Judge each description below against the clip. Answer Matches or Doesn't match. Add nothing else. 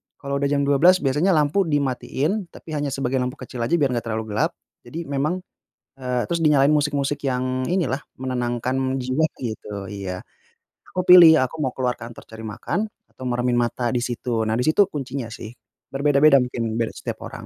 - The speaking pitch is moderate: Doesn't match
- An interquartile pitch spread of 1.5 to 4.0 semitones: Matches